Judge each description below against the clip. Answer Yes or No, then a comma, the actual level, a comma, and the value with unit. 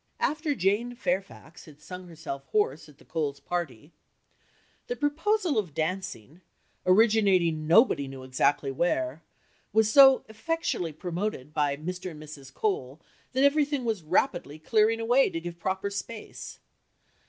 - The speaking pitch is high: No, medium, 180 Hz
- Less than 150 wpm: Yes, slow, 135 wpm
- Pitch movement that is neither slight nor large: No, wide, 6.8 semitones